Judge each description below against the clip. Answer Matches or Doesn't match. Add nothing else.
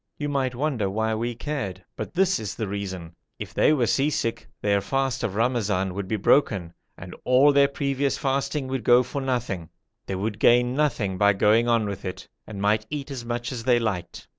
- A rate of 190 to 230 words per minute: Matches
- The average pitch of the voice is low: Matches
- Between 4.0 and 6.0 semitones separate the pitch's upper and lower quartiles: Matches